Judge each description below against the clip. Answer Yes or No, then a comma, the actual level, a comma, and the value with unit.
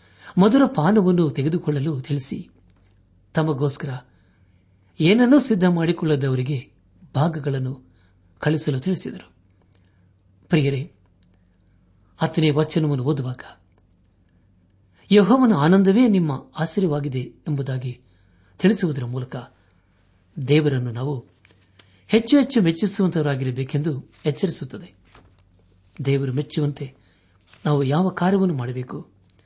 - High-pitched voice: No, low, 135 Hz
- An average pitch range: No, wide, 8.9 semitones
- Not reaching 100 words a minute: Yes, average, 70 wpm